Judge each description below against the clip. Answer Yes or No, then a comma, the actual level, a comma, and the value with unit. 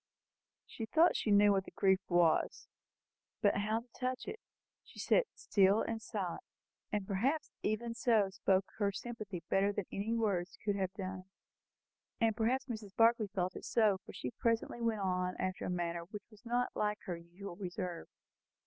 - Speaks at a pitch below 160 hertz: No, high, 205 Hz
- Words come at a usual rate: Yes, average, 175 wpm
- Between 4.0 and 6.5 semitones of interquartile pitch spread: No, average, 3.3 semitones